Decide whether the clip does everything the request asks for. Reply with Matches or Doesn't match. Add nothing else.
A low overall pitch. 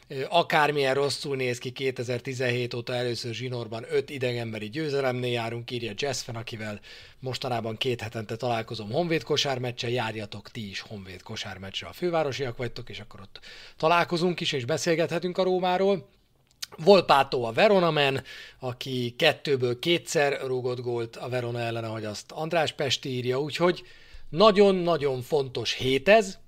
Matches